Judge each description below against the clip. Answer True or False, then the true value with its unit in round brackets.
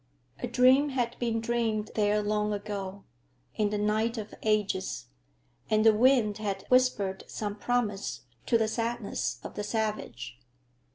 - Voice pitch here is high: True (215 Hz)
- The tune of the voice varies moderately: False (2.2 semitones)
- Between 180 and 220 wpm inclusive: False (145 wpm)